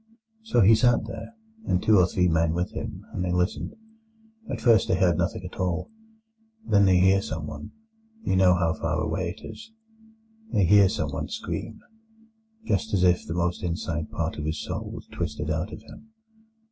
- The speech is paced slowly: No, average, 175 wpm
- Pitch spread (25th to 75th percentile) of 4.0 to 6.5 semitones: Yes, wide, 5.6 semitones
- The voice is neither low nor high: No, very low, 90 Hz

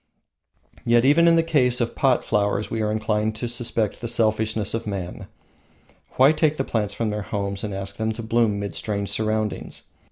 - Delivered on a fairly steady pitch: Yes, narrow, 2.3 semitones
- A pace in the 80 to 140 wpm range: No, average, 190 wpm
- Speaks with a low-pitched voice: Yes, low, 110 Hz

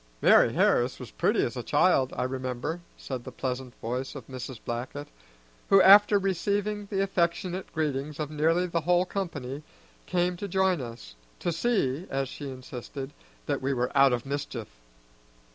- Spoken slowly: No, average, 160 wpm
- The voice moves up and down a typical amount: No, wide, 5.8 semitones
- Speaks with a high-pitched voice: No, medium, 145 Hz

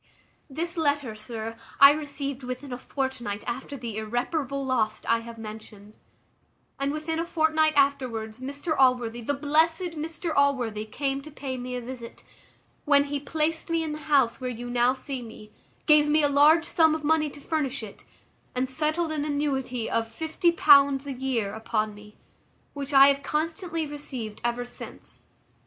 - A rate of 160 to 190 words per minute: Yes, average, 165 wpm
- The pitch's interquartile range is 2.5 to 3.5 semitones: No, average, 4.1 semitones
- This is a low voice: No, very high, 275 Hz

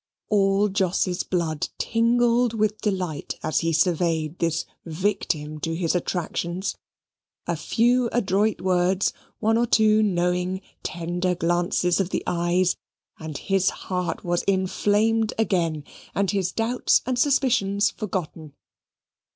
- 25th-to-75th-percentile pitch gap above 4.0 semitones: No, average, 3.6 semitones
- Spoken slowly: Yes, slow, 120 wpm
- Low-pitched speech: No, medium, 185 Hz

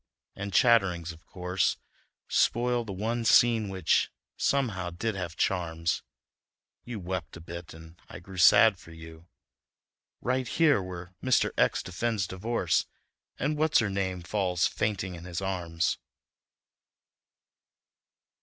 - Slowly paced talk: Yes, slow, 125 wpm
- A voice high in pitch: No, very low, 95 Hz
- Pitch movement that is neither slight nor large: Yes, average, 4.7 semitones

